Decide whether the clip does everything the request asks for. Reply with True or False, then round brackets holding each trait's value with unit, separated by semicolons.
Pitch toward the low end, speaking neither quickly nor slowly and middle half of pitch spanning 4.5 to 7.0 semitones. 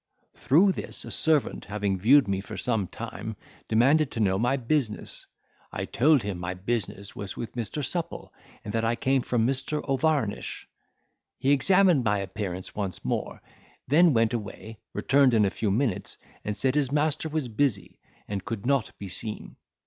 True (115 Hz; 170 wpm; 5.4 semitones)